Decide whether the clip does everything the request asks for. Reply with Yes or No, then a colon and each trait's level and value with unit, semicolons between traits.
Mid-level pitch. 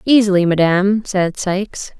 No: high, 195 Hz